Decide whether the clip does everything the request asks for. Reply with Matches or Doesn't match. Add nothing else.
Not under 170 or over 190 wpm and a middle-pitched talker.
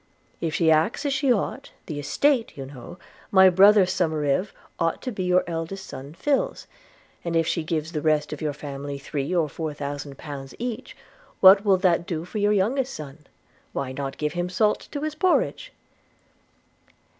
Matches